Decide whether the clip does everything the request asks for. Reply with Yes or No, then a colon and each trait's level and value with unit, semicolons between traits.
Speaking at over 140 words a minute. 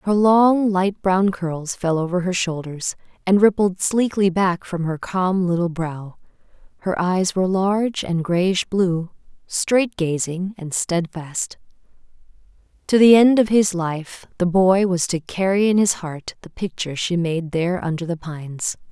Yes: average, 160 wpm